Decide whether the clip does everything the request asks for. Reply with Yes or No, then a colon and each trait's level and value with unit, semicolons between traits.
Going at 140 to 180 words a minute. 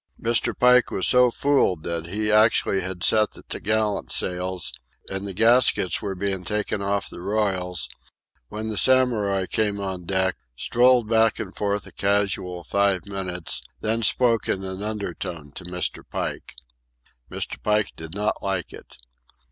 Yes: average, 155 wpm